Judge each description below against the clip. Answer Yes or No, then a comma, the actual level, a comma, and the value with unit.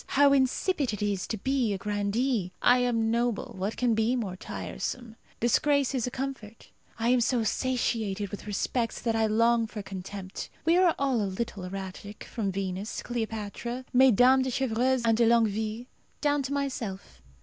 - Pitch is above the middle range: Yes, high, 230 Hz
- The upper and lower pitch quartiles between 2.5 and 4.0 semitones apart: Yes, average, 3.7 semitones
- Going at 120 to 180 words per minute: Yes, average, 170 wpm